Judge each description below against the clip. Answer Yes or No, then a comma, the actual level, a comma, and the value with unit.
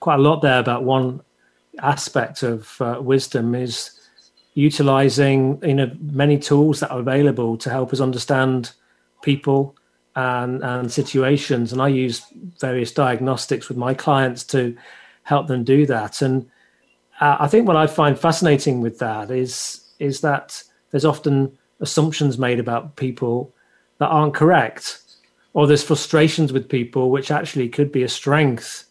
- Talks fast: No, average, 150 wpm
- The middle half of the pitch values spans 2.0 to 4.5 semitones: Yes, narrow, 2.6 semitones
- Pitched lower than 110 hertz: No, low, 135 Hz